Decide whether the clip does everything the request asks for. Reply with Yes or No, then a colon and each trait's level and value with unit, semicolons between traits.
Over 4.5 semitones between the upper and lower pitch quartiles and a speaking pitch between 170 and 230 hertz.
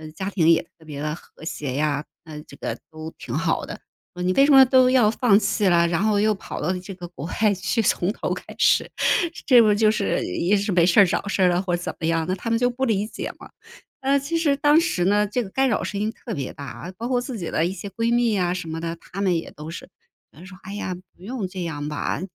Yes: average, 5.0 semitones; high, 190 Hz